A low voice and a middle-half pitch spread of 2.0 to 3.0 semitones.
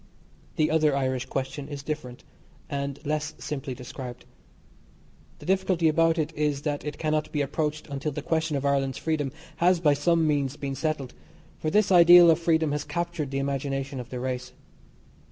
No: medium, 150 Hz; average, 2.7 semitones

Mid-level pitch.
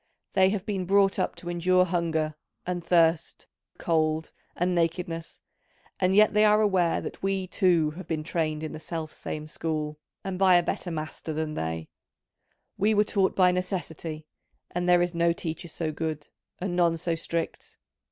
Yes: medium, 170 Hz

